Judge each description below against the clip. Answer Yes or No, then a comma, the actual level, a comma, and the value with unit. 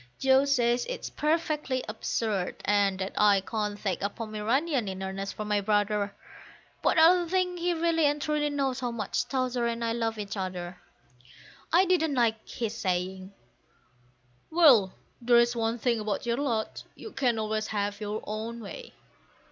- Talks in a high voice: Yes, high, 230 Hz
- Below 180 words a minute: Yes, average, 165 wpm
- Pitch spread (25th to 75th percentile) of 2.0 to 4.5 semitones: No, average, 5.2 semitones